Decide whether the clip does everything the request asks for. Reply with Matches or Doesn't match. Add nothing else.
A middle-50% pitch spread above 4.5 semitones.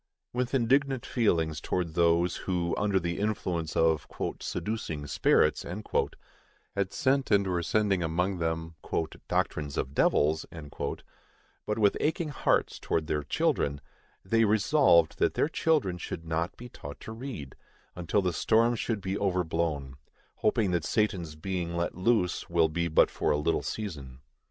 Matches